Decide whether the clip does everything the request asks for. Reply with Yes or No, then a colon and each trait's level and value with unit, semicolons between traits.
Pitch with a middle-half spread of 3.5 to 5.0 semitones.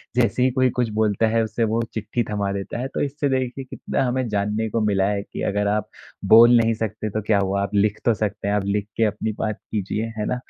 No: narrow, 2.4 semitones